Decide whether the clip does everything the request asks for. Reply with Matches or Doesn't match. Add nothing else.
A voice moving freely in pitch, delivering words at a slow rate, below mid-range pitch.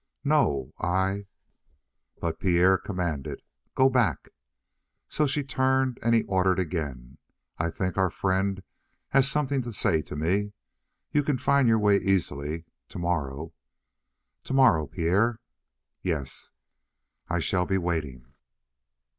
Matches